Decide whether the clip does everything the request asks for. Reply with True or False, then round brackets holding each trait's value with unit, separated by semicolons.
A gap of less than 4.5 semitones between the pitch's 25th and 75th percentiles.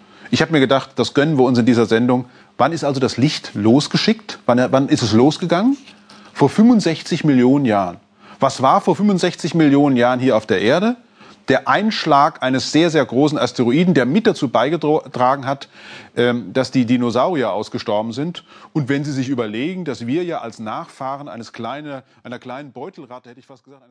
False (4.9 semitones)